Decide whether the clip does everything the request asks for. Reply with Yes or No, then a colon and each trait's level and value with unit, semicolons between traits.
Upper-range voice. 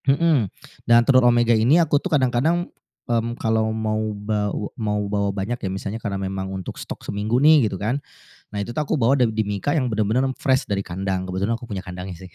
No: low, 110 Hz